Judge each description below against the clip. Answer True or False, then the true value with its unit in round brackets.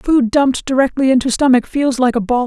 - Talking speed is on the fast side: True (220 wpm)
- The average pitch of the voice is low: False (260 Hz)